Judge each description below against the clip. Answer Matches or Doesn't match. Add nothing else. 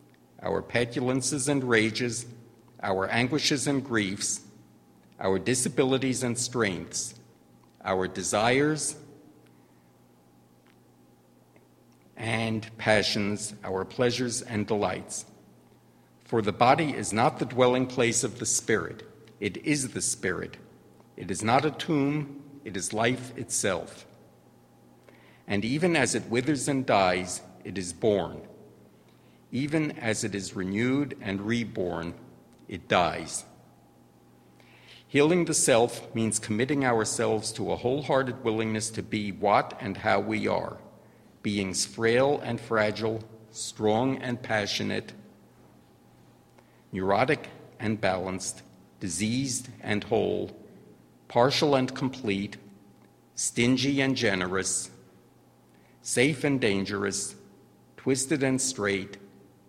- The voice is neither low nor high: Doesn't match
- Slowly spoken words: Matches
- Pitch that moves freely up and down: Doesn't match